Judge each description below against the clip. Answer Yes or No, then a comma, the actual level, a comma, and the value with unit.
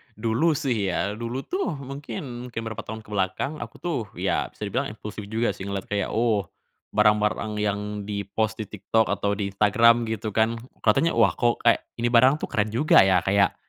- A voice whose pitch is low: Yes, low, 110 Hz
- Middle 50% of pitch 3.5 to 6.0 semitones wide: No, average, 2.7 semitones